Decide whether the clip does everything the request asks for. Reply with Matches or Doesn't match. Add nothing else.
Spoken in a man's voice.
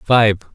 Matches